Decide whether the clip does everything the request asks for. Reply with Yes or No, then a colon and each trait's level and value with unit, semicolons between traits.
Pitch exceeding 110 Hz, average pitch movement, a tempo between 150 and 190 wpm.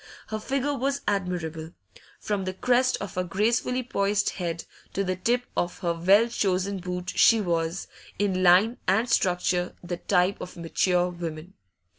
Yes: medium, 185 Hz; average, 3.4 semitones; average, 155 wpm